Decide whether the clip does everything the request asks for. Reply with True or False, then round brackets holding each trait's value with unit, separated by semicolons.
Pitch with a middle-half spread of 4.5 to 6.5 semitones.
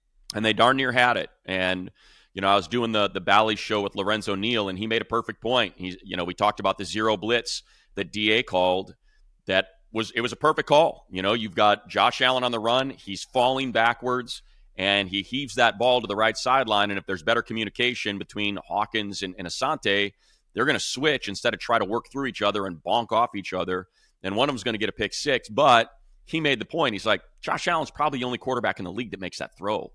False (3.5 semitones)